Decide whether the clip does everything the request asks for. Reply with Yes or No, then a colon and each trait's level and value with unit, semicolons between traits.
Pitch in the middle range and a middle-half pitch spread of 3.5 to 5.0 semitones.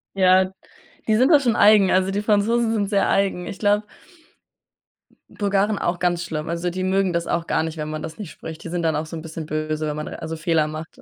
Yes: medium, 180 Hz; average, 4.0 semitones